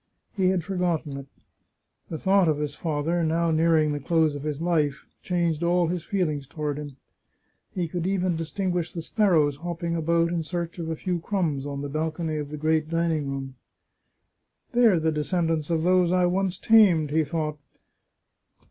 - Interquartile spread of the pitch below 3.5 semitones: Yes, narrow, 2.6 semitones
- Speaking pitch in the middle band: Yes, medium, 165 Hz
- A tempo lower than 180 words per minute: No, average, 185 wpm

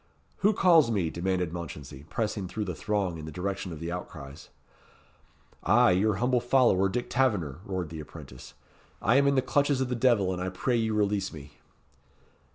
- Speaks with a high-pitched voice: No, very low, 95 Hz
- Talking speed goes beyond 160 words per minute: Yes, average, 180 wpm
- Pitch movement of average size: No, wide, 6.1 semitones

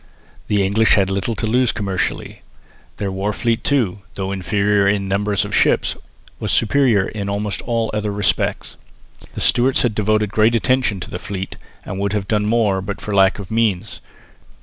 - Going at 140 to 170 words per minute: No, average, 180 wpm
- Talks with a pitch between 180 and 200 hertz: No, low, 105 Hz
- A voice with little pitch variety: Yes, narrow, 2.2 semitones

